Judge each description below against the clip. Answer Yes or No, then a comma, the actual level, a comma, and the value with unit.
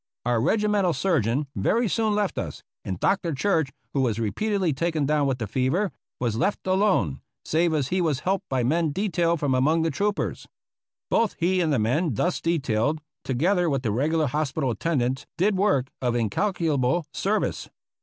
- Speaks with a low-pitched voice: No, medium, 155 Hz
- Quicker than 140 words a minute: Yes, average, 180 wpm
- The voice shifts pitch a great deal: Yes, wide, 6.3 semitones